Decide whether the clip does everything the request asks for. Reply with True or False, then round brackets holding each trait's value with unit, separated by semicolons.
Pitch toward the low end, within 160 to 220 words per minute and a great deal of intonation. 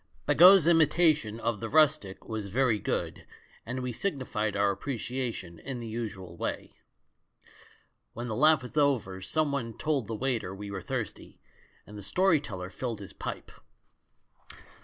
False (120 Hz; 145 wpm; 5.7 semitones)